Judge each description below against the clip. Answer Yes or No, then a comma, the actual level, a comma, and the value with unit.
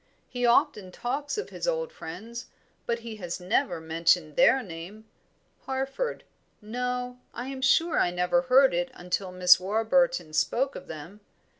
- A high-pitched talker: Yes, high, 230 Hz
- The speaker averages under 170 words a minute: Yes, average, 150 wpm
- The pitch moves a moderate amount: No, wide, 6.6 semitones